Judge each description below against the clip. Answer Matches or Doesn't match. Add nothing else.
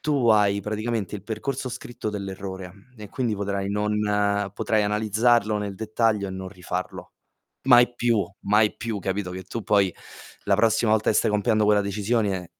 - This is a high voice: Doesn't match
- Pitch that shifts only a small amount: Matches